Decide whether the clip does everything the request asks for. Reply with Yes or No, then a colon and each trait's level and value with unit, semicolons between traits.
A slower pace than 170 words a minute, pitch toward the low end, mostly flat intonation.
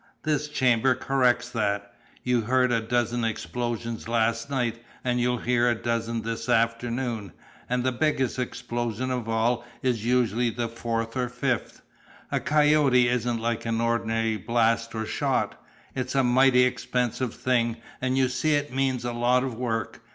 Yes: average, 160 wpm; low, 120 Hz; narrow, 1.7 semitones